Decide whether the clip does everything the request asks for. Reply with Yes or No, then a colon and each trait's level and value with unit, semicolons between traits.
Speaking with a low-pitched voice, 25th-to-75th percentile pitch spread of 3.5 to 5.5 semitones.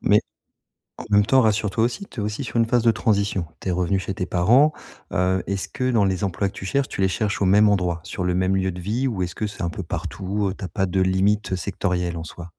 No: very low, 95 Hz; average, 2.7 semitones